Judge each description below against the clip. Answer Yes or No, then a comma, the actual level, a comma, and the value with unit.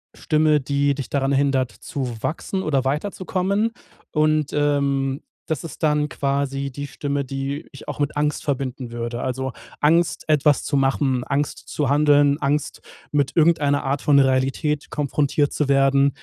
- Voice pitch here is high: No, medium, 140 Hz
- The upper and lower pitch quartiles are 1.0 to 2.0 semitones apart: Yes, narrow, 1.7 semitones